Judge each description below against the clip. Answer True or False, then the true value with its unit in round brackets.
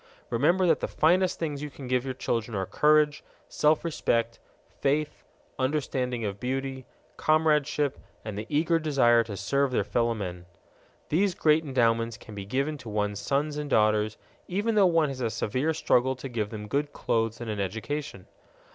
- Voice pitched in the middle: False (130 Hz)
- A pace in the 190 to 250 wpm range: False (170 wpm)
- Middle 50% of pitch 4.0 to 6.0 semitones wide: True (5.0 semitones)